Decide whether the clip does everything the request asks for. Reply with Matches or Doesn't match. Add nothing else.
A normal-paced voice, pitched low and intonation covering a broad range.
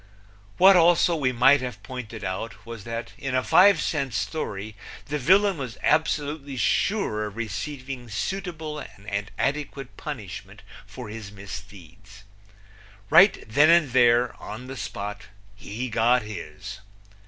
Doesn't match